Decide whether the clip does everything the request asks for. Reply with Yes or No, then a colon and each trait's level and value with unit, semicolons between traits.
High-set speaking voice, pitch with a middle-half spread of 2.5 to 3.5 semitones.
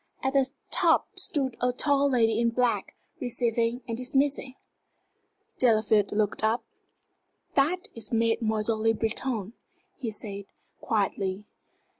Yes: high, 230 Hz; average, 2.9 semitones